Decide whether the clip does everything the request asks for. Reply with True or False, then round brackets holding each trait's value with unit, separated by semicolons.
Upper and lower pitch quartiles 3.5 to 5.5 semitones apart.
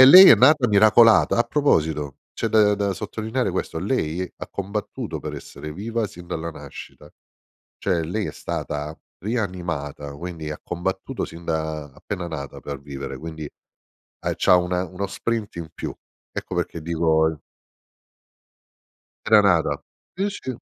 True (5.2 semitones)